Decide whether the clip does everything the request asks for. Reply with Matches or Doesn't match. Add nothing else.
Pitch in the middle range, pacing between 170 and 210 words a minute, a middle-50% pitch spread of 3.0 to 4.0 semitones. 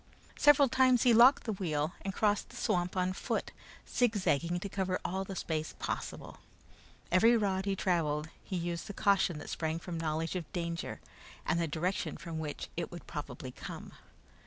Matches